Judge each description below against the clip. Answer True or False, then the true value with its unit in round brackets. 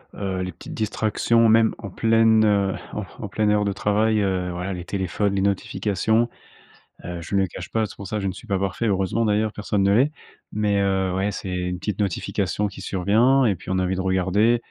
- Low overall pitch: True (100 Hz)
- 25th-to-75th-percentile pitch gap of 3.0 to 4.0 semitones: False (2.4 semitones)